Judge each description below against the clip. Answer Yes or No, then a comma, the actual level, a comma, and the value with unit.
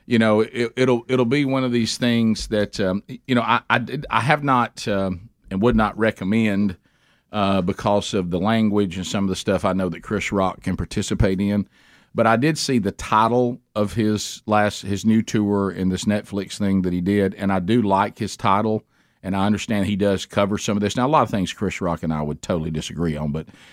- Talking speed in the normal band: No, fast, 230 wpm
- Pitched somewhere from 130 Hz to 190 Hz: No, low, 105 Hz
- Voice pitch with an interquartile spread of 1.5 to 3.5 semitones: Yes, average, 2.8 semitones